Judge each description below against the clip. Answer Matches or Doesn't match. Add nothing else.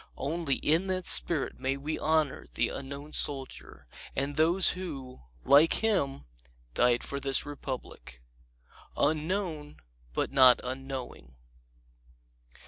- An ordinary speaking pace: Doesn't match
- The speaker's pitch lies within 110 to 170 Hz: Matches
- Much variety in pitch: Doesn't match